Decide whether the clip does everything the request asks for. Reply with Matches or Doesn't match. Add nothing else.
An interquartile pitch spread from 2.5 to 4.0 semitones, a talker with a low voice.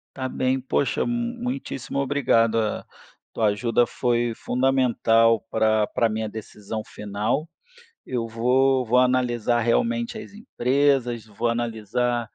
Matches